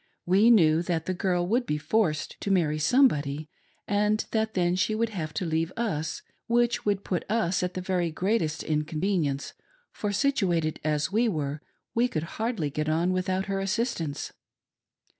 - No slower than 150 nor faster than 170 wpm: Yes, average, 165 wpm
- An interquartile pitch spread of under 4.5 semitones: No, average, 5.3 semitones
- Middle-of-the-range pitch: Yes, medium, 180 Hz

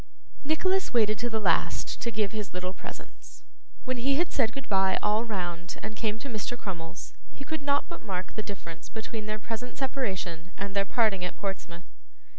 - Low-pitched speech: No, high, 215 Hz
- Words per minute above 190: No, average, 185 wpm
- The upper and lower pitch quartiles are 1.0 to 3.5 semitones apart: No, average, 4.3 semitones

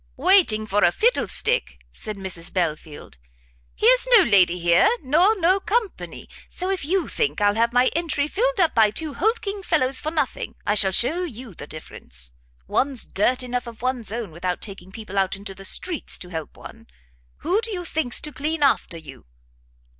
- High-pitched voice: Yes, very high, 250 Hz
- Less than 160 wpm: No, average, 180 wpm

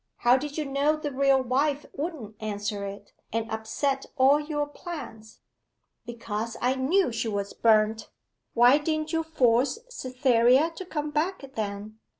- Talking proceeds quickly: No, average, 150 wpm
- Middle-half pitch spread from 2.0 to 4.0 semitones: No, average, 5.0 semitones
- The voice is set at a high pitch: Yes, very high, 260 Hz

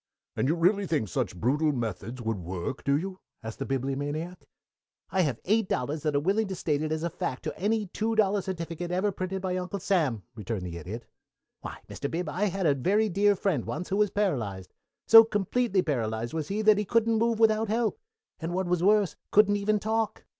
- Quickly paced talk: Yes, fast, 210 wpm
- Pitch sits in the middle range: Yes, medium, 180 Hz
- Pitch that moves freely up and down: Yes, wide, 7.1 semitones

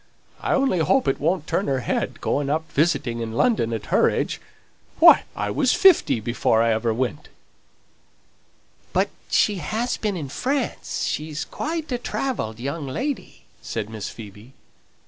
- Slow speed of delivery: No, average, 155 wpm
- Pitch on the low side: No, medium, 145 Hz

